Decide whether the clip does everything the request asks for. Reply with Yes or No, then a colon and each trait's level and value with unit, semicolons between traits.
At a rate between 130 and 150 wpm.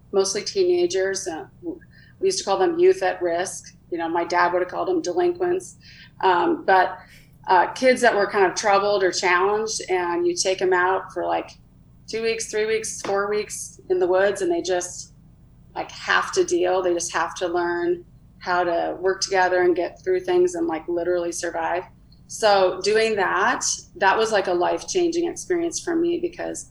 No: average, 185 wpm